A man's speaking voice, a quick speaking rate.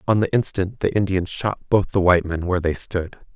Yes: male; fast, 235 wpm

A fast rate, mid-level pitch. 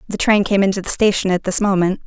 No: fast, 260 wpm; high, 195 Hz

